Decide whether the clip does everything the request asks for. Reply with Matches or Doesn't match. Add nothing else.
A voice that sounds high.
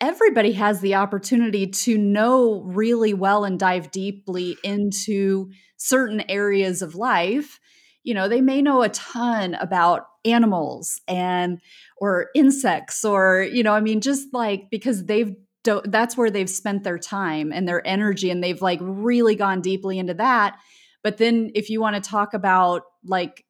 Matches